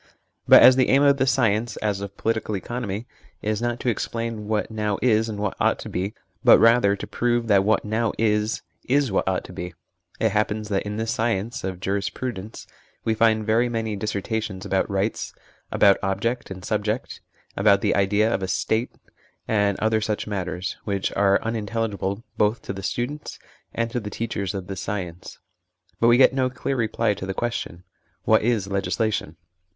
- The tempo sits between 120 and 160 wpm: No, average, 190 wpm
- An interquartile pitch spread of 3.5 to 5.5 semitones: No, average, 2.7 semitones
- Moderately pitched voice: No, low, 105 Hz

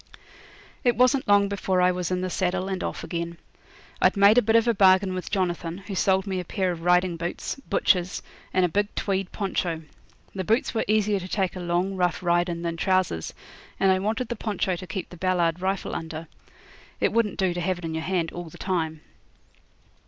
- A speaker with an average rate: No, fast, 210 wpm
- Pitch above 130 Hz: Yes, medium, 185 Hz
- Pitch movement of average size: No, narrow, 2.2 semitones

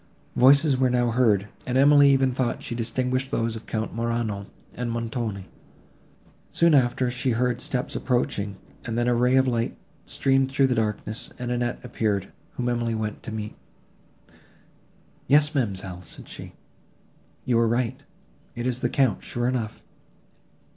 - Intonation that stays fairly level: Yes, narrow, 2.3 semitones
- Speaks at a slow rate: No, average, 155 wpm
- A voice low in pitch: Yes, low, 120 Hz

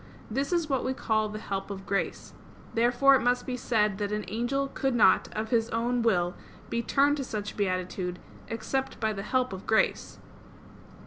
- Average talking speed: Yes, average, 185 wpm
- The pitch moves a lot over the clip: No, average, 3.8 semitones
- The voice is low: No, high, 230 Hz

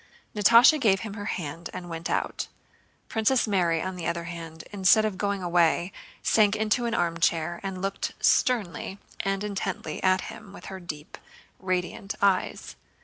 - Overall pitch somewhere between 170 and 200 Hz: Yes, high, 190 Hz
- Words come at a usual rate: Yes, average, 155 wpm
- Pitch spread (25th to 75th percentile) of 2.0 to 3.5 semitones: Yes, average, 3.2 semitones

